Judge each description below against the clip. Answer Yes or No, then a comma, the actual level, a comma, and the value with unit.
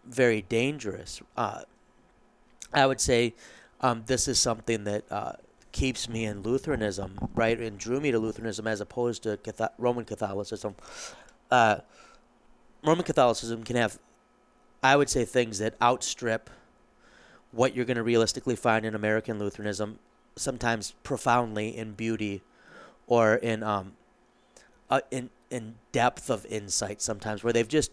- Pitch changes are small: Yes, narrow, 2.3 semitones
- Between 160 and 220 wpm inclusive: No, average, 140 wpm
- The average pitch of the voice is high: No, low, 115 Hz